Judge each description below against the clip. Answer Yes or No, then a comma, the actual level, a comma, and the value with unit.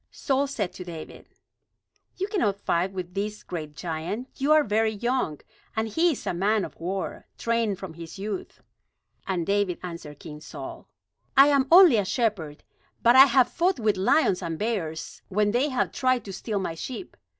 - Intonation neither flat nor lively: No, wide, 6.1 semitones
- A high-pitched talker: Yes, high, 205 Hz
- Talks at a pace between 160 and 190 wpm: Yes, average, 180 wpm